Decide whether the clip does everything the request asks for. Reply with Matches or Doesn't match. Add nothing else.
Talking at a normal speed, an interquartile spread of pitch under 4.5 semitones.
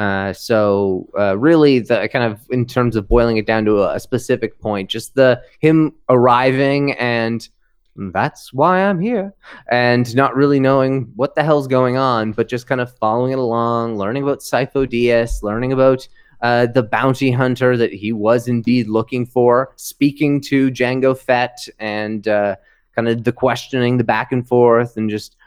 Matches